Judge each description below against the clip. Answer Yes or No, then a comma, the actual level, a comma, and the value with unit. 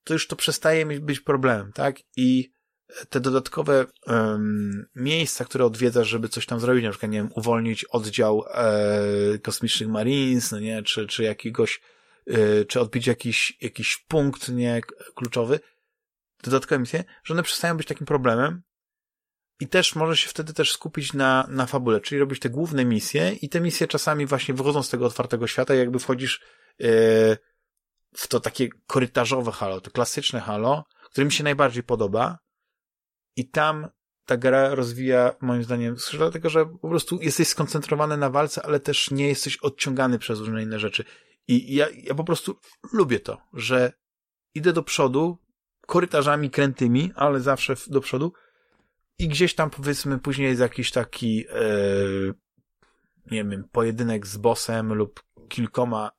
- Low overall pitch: Yes, low, 130 Hz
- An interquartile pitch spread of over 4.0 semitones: Yes, average, 4.5 semitones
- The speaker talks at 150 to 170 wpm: Yes, average, 155 wpm